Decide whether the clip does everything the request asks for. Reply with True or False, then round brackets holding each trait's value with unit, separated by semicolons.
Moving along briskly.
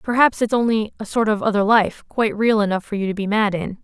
True (250 wpm)